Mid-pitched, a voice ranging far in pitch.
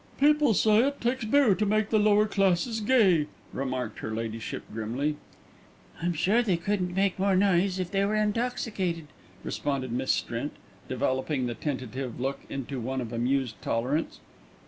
Yes: medium, 175 Hz; wide, 8.3 semitones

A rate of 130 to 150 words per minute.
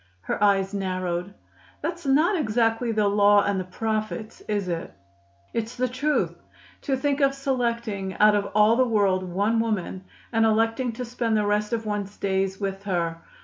No: average, 170 wpm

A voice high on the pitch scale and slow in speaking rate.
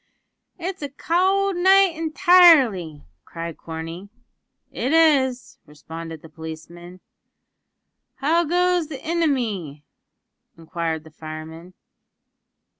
Yes: high, 235 Hz; slow, 90 wpm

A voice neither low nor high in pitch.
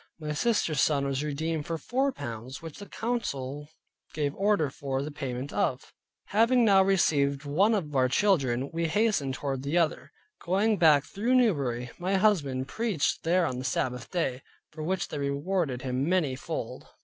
Yes: medium, 150 Hz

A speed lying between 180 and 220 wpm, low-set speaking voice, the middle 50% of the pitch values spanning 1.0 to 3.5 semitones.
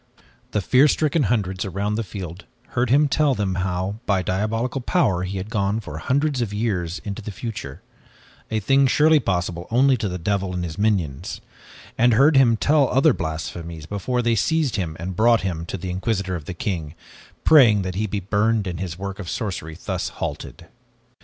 No: average, 190 wpm; low, 100 Hz; average, 4.6 semitones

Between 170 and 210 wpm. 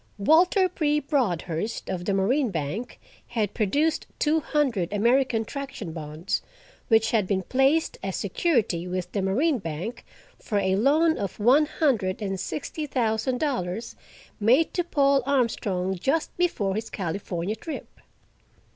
No: average, 140 wpm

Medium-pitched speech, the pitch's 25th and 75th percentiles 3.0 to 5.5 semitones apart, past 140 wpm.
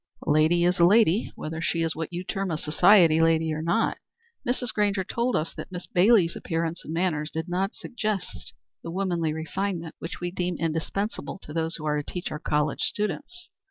Yes: medium, 170 Hz; average, 3.4 semitones; average, 195 wpm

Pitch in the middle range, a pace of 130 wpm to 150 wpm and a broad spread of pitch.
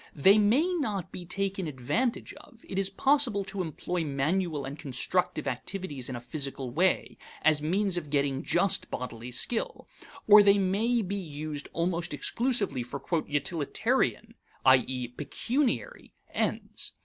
Yes: medium, 175 Hz; slow, 135 wpm; wide, 6.3 semitones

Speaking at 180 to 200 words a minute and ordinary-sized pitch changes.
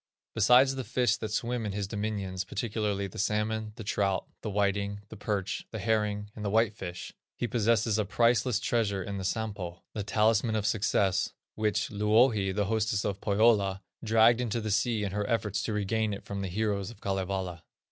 No: average, 190 wpm; narrow, 2.0 semitones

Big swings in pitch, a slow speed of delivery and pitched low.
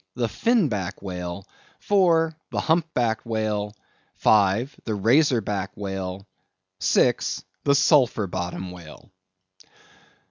Yes: wide, 6.5 semitones; slow, 110 wpm; low, 110 Hz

